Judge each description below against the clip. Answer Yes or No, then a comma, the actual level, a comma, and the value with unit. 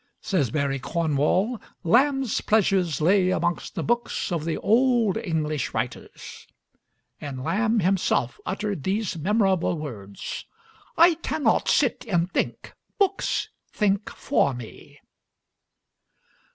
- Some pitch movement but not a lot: No, wide, 6.4 semitones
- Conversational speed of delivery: No, slow, 110 wpm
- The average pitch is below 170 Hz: No, high, 190 Hz